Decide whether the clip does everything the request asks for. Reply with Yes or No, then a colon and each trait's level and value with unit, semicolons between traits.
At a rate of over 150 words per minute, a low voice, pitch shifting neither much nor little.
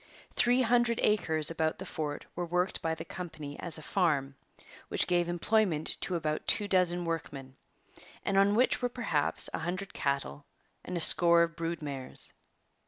No: average, 170 wpm; medium, 170 Hz; average, 3.7 semitones